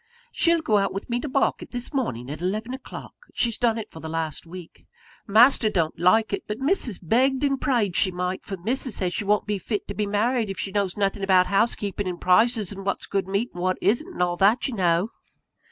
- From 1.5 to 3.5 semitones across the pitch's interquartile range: No, average, 4.4 semitones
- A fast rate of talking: Yes, fast, 230 wpm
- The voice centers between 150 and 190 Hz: No, high, 205 Hz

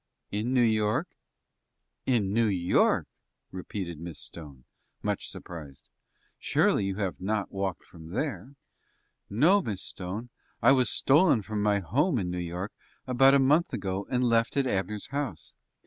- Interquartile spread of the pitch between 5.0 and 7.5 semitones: Yes, wide, 5.4 semitones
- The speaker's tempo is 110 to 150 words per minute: Yes, average, 145 wpm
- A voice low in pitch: Yes, low, 105 Hz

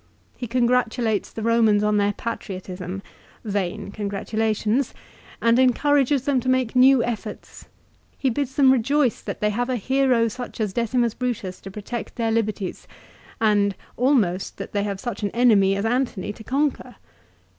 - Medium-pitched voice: No, high, 230 Hz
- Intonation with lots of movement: No, average, 3.6 semitones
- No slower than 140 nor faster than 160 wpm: Yes, average, 155 wpm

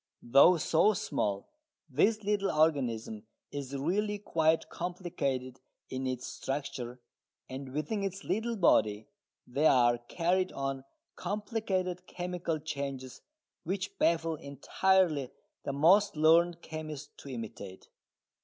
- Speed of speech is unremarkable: No, slow, 110 wpm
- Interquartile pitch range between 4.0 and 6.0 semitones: Yes, wide, 5.6 semitones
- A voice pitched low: No, medium, 155 Hz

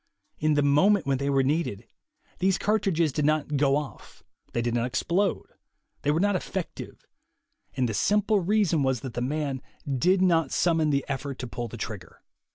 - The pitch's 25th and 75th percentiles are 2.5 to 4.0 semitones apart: No, average, 5.1 semitones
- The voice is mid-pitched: Yes, medium, 150 Hz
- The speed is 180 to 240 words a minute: Yes, average, 185 wpm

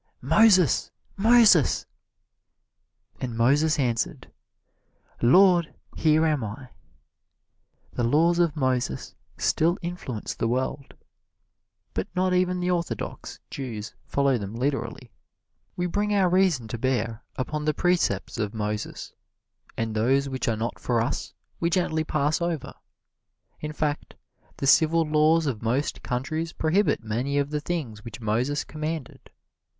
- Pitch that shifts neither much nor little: No, wide, 5.9 semitones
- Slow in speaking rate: Yes, slow, 130 wpm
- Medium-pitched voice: Yes, medium, 145 Hz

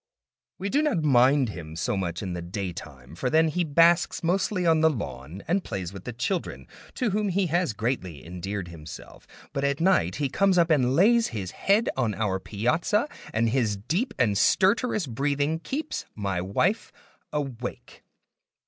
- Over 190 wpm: No, average, 170 wpm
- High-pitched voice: No, low, 135 Hz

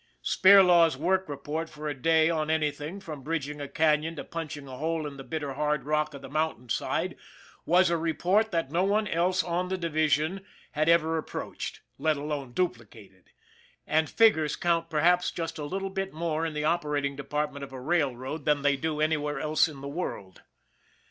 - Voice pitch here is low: No, medium, 155 Hz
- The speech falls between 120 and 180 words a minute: No, average, 190 wpm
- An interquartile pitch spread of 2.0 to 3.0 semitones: Yes, narrow, 2.5 semitones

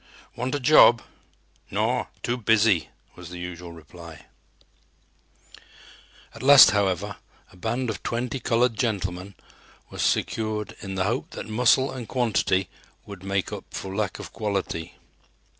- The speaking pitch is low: Yes, low, 105 Hz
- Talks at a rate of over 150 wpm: No, slow, 135 wpm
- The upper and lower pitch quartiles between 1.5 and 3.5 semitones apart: No, average, 4.2 semitones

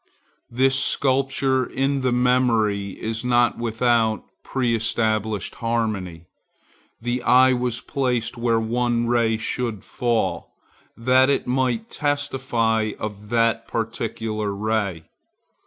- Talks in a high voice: No, low, 115 Hz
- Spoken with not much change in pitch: Yes, narrow, 2.3 semitones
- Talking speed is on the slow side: Yes, slow, 105 wpm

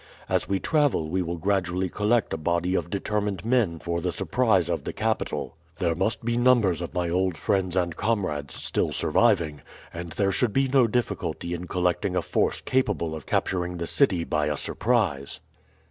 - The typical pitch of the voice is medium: No, very low, 90 Hz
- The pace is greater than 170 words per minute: Yes, average, 180 wpm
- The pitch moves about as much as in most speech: Yes, average, 4.4 semitones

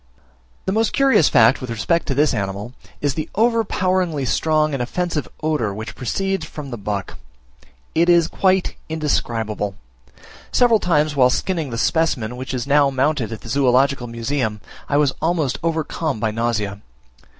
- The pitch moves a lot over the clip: Yes, wide, 5.7 semitones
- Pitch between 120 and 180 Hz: Yes, medium, 140 Hz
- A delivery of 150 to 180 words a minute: Yes, average, 155 wpm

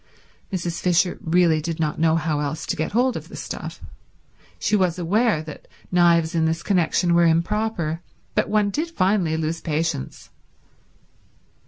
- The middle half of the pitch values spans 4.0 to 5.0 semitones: No, average, 2.8 semitones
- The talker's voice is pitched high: No, medium, 170 Hz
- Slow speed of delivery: No, average, 155 wpm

